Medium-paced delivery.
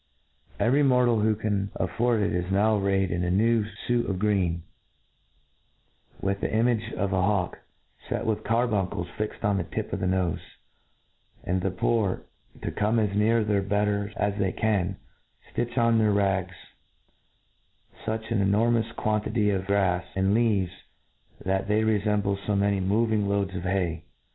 Yes: average, 160 wpm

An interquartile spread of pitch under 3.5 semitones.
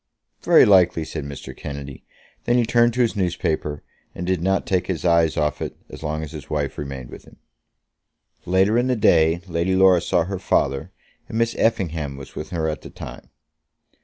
No: average, 4.0 semitones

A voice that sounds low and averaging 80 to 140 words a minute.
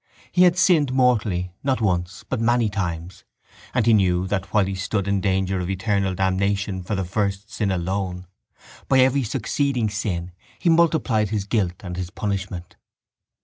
No: low, 100 Hz; average, 165 wpm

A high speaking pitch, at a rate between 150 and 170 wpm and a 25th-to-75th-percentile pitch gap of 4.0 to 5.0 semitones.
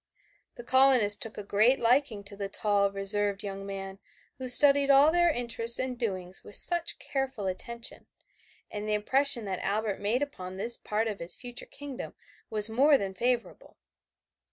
Yes: high, 225 Hz; average, 165 wpm; average, 4.5 semitones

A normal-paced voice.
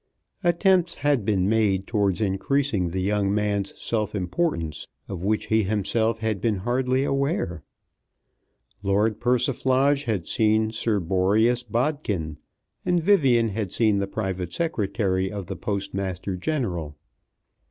No: slow, 125 wpm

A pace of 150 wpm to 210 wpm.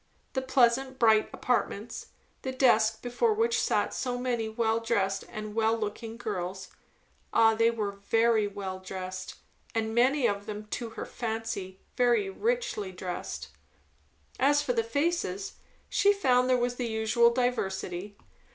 No: average, 140 wpm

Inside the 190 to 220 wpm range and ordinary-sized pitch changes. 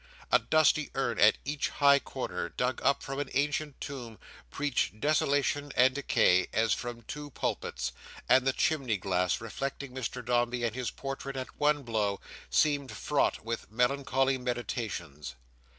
No: average, 150 wpm; average, 3.7 semitones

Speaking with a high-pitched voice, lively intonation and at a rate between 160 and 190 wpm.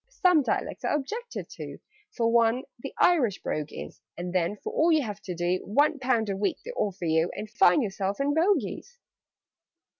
Yes: high, 230 Hz; wide, 7.8 semitones; average, 185 wpm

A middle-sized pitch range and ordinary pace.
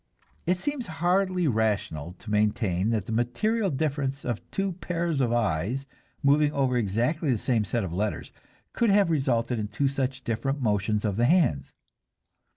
No: wide, 6.7 semitones; average, 160 wpm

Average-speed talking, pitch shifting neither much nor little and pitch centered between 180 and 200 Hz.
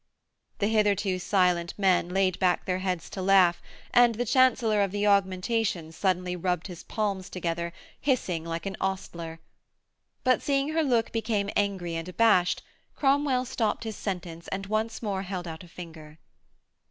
Yes: average, 155 wpm; average, 3.5 semitones; high, 190 Hz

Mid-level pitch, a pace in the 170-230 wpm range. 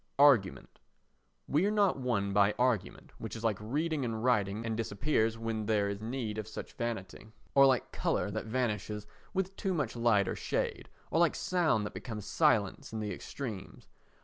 No: low, 115 Hz; average, 175 wpm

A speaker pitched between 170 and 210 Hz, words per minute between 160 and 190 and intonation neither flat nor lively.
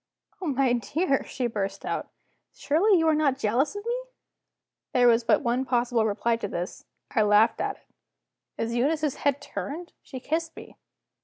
No: very high, 260 Hz; average, 170 wpm; average, 4.9 semitones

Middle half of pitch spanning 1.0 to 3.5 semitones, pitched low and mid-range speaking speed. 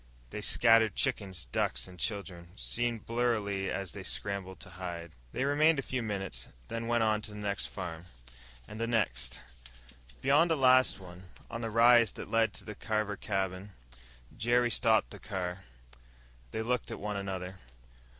No: average, 3.9 semitones; low, 105 Hz; average, 170 wpm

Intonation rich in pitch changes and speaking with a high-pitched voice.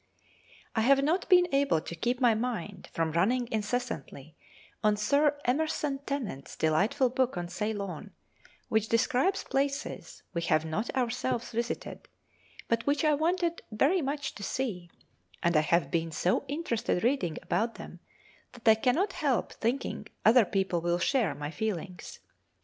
Yes: wide, 7.4 semitones; high, 230 Hz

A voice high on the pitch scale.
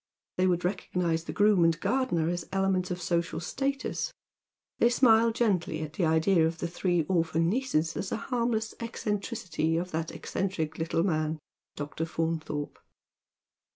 No: medium, 175 Hz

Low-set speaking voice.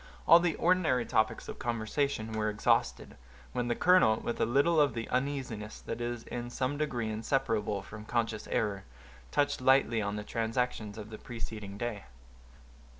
Yes: low, 115 Hz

